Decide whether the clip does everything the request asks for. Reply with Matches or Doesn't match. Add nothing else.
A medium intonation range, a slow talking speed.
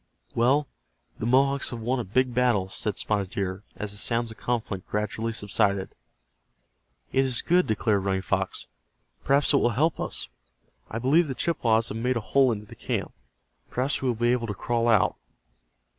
Doesn't match